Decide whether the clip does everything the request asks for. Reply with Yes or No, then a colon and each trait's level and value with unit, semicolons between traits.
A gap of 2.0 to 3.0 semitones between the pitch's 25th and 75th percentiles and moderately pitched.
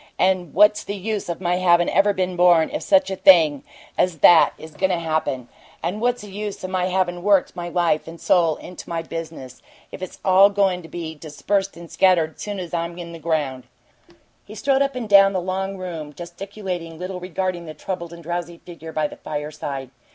Yes: average, 2.7 semitones; medium, 175 Hz